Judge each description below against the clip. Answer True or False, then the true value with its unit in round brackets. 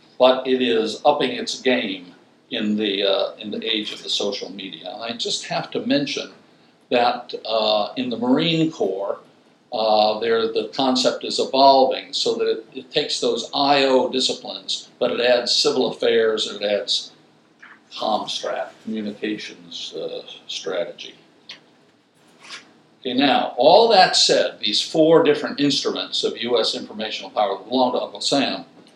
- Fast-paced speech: False (145 wpm)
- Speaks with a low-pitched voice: False (145 Hz)